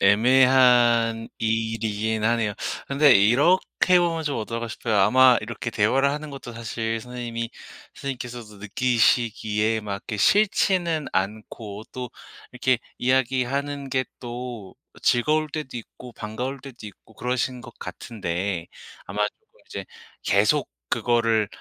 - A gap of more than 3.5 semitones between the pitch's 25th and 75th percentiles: No, average, 3.1 semitones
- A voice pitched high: No, low, 120 Hz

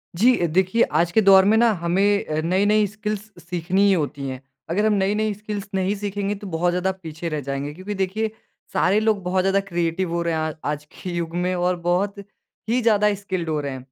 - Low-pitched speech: No, high, 190 Hz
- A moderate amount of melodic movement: Yes, average, 3.4 semitones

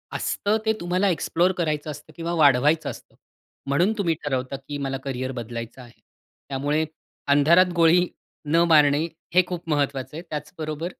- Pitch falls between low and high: Yes, medium, 150 Hz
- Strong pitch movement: No, average, 3.6 semitones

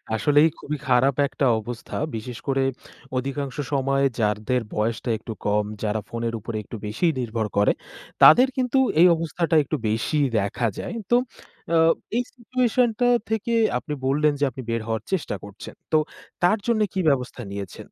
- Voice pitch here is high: No, low, 135 Hz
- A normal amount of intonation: No, wide, 6.6 semitones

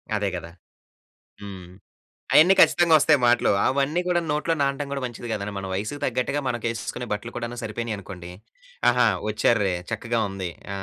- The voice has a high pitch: No, low, 120 Hz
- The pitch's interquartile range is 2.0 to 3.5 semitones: No, average, 5.2 semitones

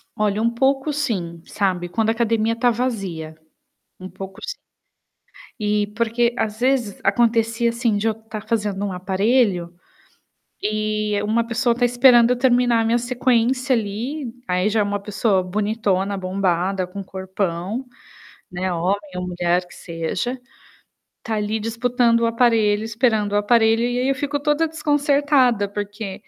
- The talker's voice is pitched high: Yes, high, 220 Hz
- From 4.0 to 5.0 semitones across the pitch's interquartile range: No, average, 3.5 semitones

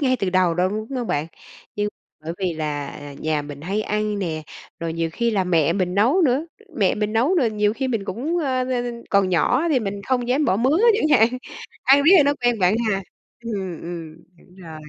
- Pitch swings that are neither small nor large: No, wide, 6.1 semitones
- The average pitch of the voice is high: Yes, high, 205 Hz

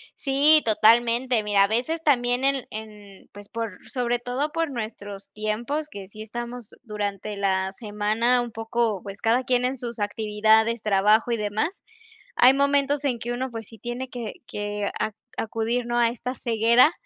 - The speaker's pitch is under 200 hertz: No, high, 230 Hz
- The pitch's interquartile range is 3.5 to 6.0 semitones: No, average, 2.8 semitones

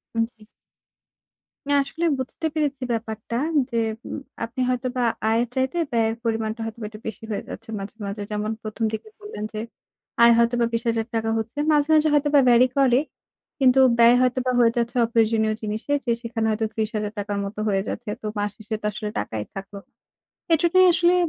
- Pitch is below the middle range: No, high, 230 Hz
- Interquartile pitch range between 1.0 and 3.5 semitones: Yes, average, 2.9 semitones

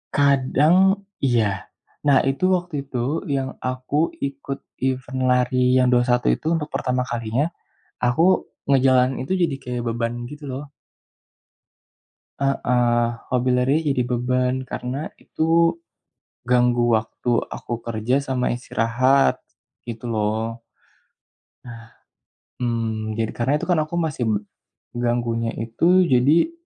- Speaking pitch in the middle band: No, low, 125 Hz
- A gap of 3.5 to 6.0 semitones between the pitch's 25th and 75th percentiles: No, narrow, 2.6 semitones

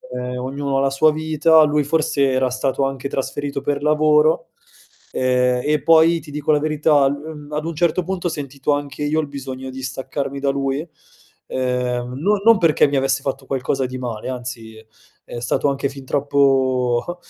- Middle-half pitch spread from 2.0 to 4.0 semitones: Yes, narrow, 2.6 semitones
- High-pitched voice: No, medium, 140 Hz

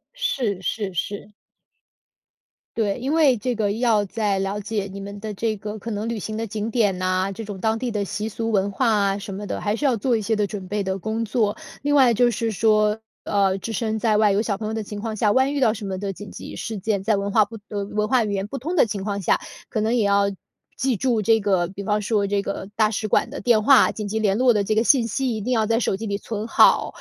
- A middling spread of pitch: No, narrow, 2.2 semitones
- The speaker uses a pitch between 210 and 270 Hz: Yes, high, 215 Hz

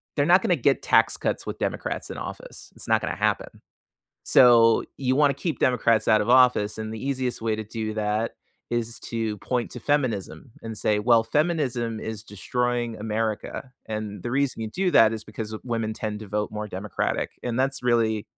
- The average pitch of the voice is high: No, low, 115 Hz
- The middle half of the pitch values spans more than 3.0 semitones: No, narrow, 2.5 semitones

